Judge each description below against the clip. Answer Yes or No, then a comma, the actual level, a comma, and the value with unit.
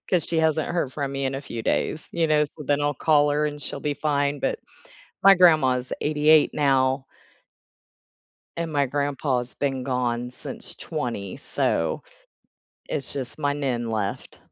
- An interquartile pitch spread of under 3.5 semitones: Yes, narrow, 2.6 semitones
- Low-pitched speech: No, medium, 145 Hz